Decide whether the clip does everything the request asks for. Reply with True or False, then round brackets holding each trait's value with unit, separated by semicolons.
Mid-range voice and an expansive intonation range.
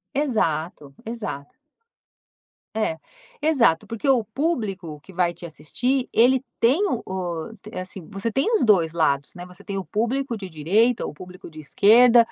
False (195 Hz; 6.0 semitones)